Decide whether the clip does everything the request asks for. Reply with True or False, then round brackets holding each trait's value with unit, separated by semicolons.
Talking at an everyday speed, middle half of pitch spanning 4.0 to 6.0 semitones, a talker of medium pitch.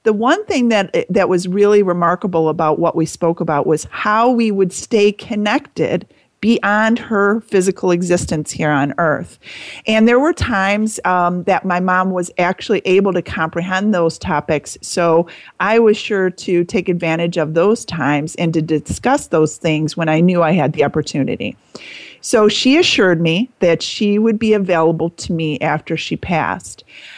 True (170 wpm; 4.4 semitones; 180 Hz)